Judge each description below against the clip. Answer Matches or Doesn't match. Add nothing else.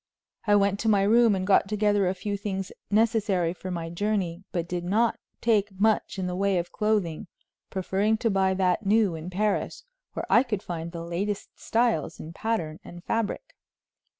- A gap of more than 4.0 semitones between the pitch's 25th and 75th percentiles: Doesn't match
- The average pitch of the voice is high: Matches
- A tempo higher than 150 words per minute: Matches